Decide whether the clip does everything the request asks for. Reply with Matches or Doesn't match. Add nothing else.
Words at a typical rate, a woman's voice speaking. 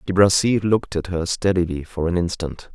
Doesn't match